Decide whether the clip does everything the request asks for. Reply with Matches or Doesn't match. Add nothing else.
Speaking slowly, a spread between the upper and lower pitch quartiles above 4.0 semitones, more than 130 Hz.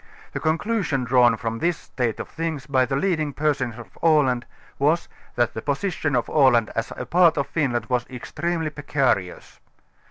Doesn't match